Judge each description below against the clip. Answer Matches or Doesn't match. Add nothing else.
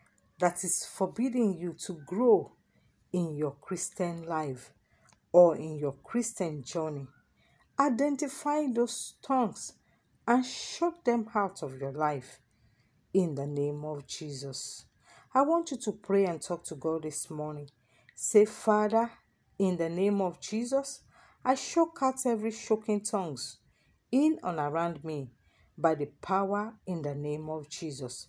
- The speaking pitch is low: Doesn't match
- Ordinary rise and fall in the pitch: Doesn't match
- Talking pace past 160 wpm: Doesn't match